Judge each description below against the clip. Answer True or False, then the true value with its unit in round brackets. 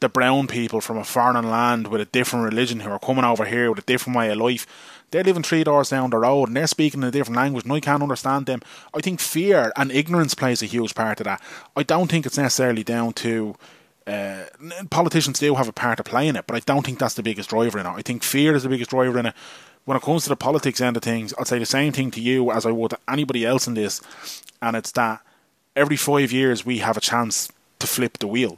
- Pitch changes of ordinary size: True (3.5 semitones)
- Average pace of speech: False (265 wpm)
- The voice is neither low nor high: False (125 Hz)